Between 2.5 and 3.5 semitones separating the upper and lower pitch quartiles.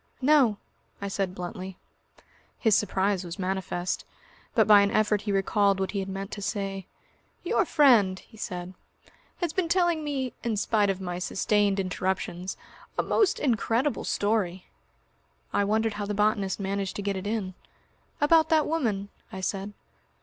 Yes: average, 2.9 semitones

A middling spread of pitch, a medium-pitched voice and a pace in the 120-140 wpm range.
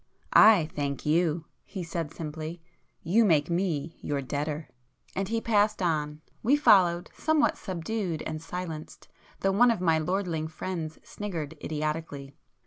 Yes: average, 3.8 semitones; medium, 165 Hz; slow, 135 wpm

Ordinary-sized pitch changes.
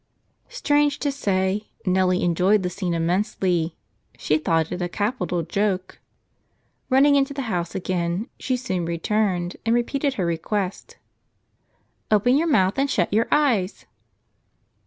No: wide, 6.0 semitones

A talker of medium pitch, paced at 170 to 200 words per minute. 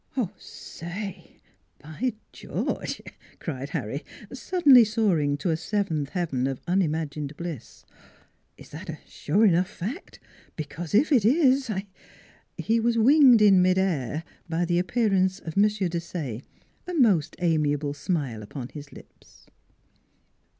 No: medium, 180 Hz; slow, 135 wpm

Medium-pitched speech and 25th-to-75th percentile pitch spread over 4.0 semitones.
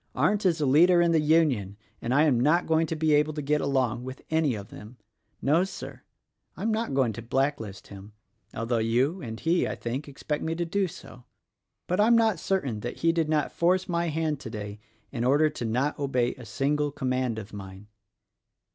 Yes: medium, 145 Hz; average, 5.3 semitones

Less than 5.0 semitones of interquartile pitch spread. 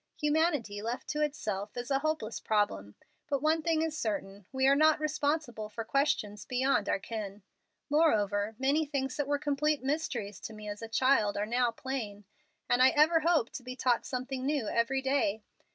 No: wide, 5.5 semitones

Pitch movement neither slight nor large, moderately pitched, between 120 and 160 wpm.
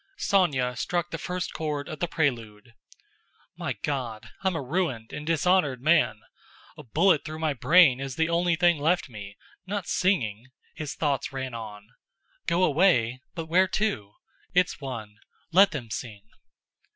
No: wide, 6.3 semitones; medium, 150 Hz; average, 145 wpm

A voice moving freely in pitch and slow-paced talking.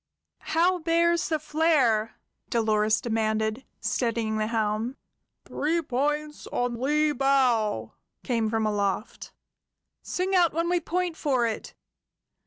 Yes: wide, 6.3 semitones; slow, 115 wpm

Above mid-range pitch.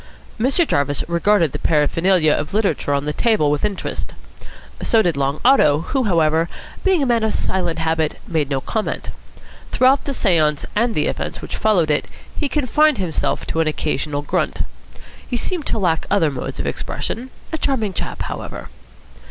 No: medium, 175 Hz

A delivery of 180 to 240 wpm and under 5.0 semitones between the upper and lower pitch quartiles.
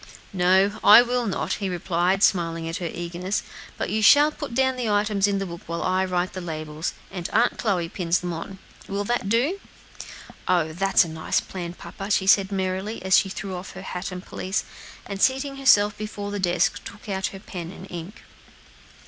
Yes: average, 195 wpm; average, 2.8 semitones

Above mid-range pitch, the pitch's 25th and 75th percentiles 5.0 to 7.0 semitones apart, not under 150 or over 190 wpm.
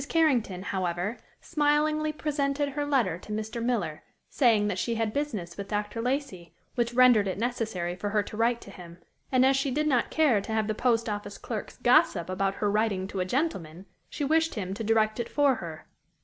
No: high, 225 Hz; average, 5.3 semitones; average, 200 wpm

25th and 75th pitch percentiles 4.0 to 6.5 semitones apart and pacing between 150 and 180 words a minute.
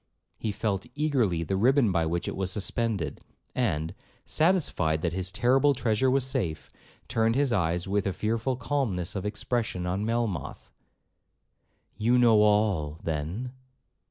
No: wide, 5.5 semitones; average, 140 wpm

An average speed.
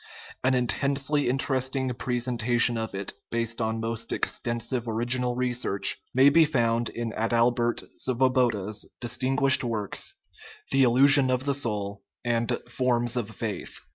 No: slow, 125 wpm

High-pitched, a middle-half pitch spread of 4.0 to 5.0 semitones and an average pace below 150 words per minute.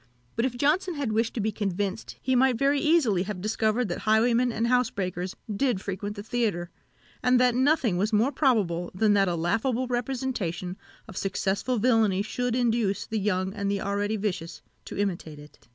No: high, 215 Hz; average, 4.4 semitones; average, 180 wpm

